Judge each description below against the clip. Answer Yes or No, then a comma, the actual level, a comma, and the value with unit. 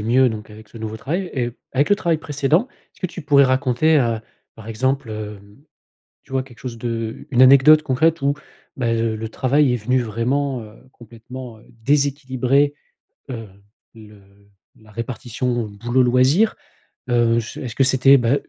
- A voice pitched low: Yes, low, 125 Hz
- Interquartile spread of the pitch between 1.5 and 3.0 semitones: No, average, 3.4 semitones